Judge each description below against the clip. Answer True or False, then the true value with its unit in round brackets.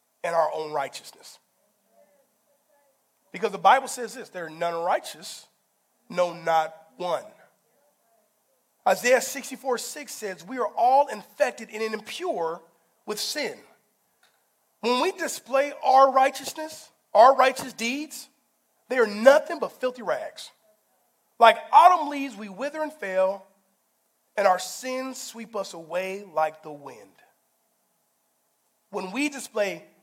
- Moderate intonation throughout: False (6.7 semitones)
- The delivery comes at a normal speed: False (120 wpm)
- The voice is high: True (240 Hz)